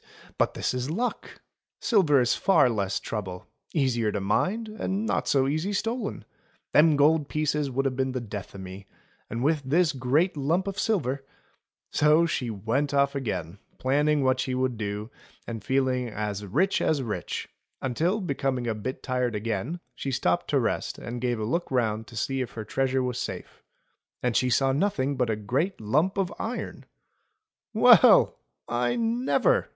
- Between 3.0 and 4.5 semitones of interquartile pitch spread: No, average, 4.9 semitones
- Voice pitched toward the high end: No, low, 130 Hz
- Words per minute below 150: No, average, 175 wpm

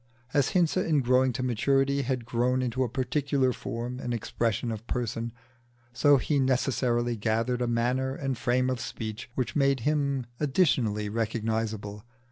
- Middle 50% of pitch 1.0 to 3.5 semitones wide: Yes, average, 2.7 semitones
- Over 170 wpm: No, average, 150 wpm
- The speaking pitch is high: No, low, 125 Hz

